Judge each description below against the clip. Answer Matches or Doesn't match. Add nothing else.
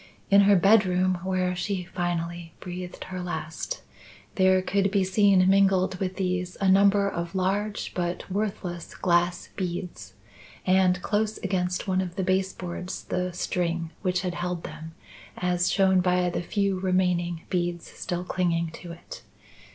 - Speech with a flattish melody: Matches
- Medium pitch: Matches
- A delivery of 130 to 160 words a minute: Matches